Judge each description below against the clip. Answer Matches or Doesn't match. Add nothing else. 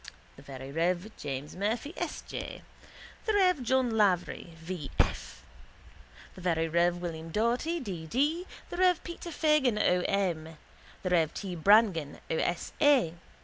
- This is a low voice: Doesn't match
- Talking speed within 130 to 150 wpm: Matches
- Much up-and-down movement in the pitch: Matches